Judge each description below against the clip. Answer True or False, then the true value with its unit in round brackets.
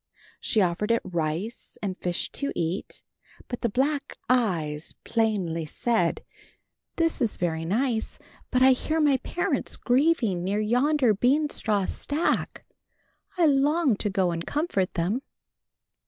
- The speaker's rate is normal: False (130 wpm)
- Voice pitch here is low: False (225 Hz)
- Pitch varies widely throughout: True (7.1 semitones)